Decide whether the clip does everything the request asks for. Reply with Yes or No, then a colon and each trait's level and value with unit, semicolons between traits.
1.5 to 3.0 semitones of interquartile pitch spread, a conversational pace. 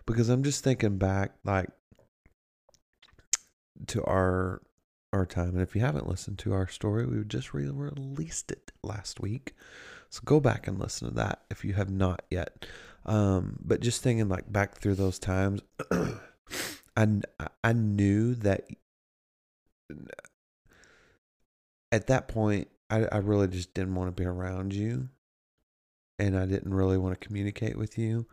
No: average, 3.4 semitones; average, 155 wpm